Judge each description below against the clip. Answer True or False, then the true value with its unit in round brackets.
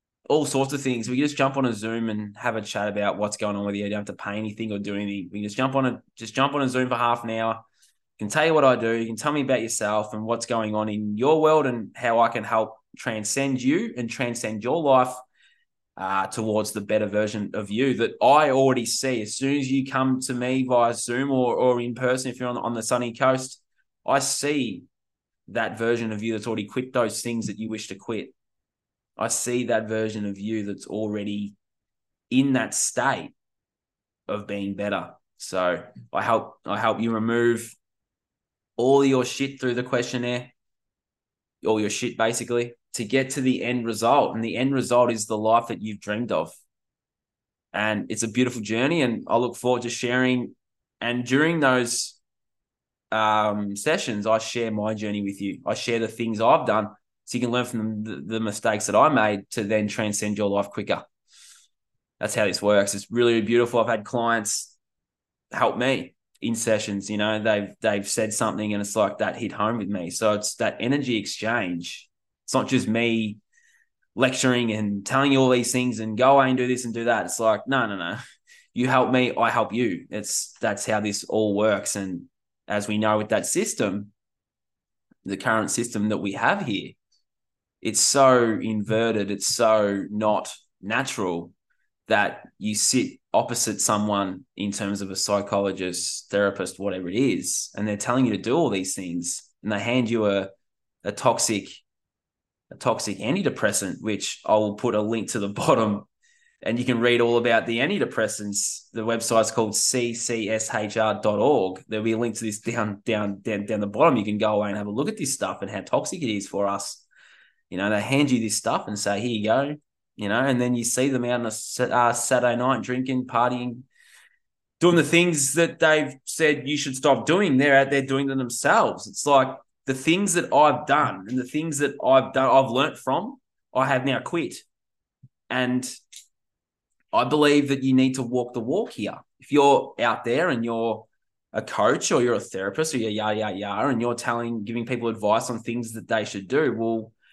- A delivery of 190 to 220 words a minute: True (200 wpm)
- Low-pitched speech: True (115 Hz)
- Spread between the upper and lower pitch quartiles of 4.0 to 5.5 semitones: False (3.2 semitones)